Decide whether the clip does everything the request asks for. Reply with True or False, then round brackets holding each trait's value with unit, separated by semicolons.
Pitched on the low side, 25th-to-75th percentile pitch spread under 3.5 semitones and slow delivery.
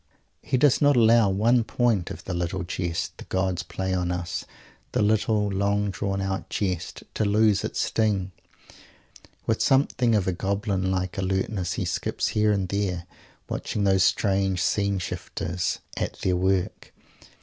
False (95 Hz; 2.4 semitones; 155 wpm)